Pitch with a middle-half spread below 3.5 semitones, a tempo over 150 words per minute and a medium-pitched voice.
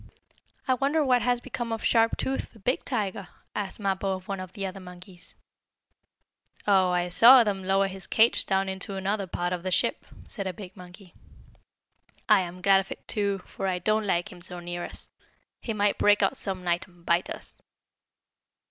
No: narrow, 2.6 semitones; average, 190 wpm; high, 195 Hz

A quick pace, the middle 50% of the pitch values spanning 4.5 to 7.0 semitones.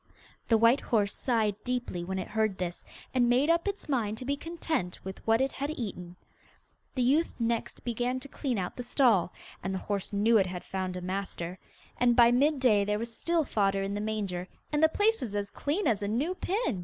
Yes: fast, 215 wpm; average, 5.2 semitones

